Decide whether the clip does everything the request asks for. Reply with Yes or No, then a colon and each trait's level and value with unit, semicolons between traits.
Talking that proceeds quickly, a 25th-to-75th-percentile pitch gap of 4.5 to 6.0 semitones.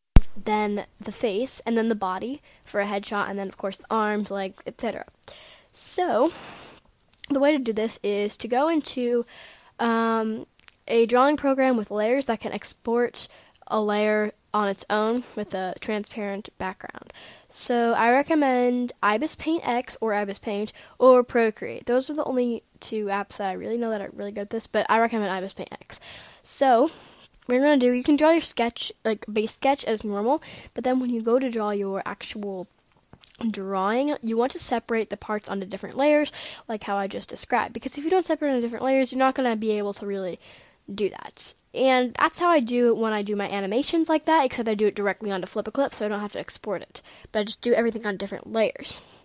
No: fast, 210 wpm; average, 3.6 semitones